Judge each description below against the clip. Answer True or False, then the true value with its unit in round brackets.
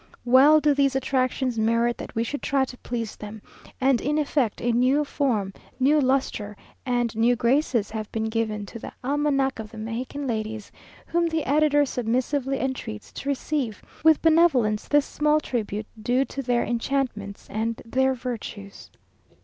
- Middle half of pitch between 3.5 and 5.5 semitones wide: True (3.8 semitones)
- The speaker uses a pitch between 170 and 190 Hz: False (250 Hz)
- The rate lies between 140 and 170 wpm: True (160 wpm)